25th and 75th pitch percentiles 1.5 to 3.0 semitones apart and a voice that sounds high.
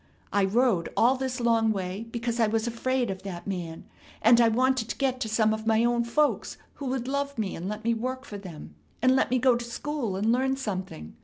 No: average, 3.7 semitones; high, 230 Hz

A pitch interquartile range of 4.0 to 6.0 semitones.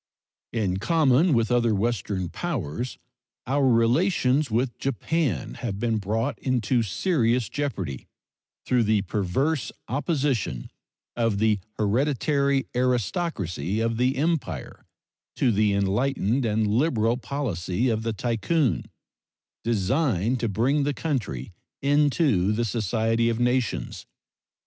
Yes: average, 4.5 semitones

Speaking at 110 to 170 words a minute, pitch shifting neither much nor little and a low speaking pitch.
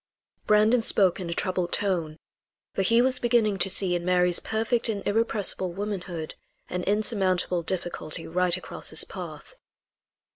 No: average, 145 wpm; average, 3.2 semitones; high, 190 Hz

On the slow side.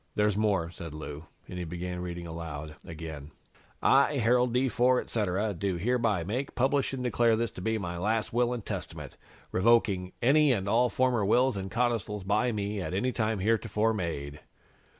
No: average, 175 wpm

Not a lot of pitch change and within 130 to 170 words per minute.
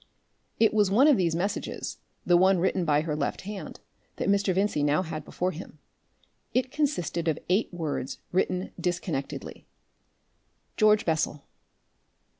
No: average, 4.0 semitones; average, 140 wpm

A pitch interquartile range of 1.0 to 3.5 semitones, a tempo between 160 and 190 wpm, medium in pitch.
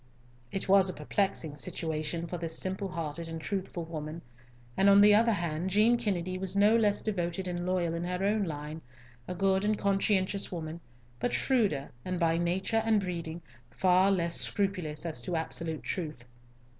Yes: average, 3.2 semitones; average, 170 wpm; medium, 180 Hz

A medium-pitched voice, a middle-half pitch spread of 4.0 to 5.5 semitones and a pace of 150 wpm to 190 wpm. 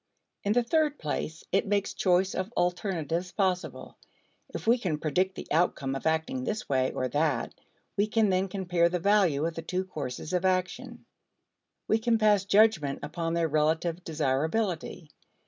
Yes: medium, 180 Hz; average, 4.3 semitones; average, 165 wpm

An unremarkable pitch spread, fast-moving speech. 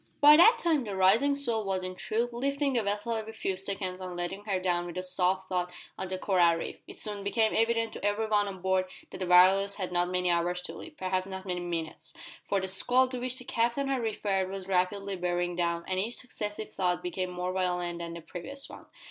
Yes: average, 3.6 semitones; fast, 230 wpm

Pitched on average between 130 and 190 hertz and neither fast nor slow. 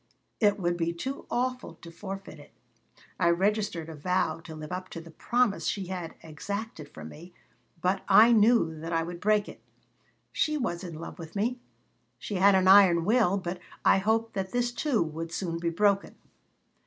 Yes: medium, 185 Hz; average, 185 wpm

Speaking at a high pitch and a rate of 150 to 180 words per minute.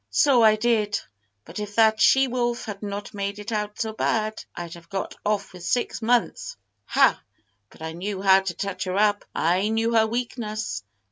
No: high, 210 Hz; average, 190 wpm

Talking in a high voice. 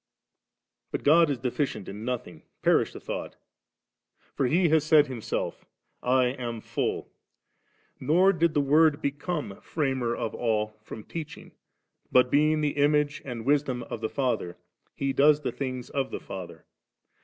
No: low, 135 Hz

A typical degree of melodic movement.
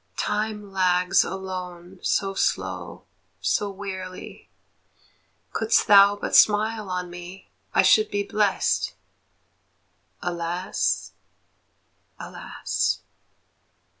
No: narrow, 2.2 semitones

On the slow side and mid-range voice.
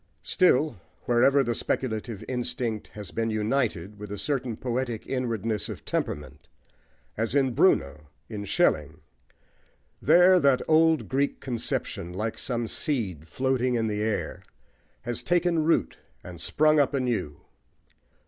No: slow, 130 wpm; low, 120 Hz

